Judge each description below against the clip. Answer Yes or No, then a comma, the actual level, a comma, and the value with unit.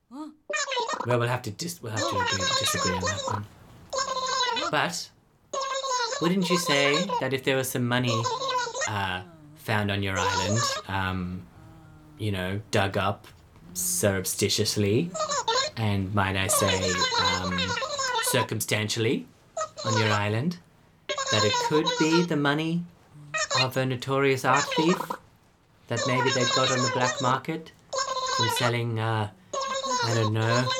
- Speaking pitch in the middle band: No, low, 130 Hz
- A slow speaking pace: Yes, slow, 130 wpm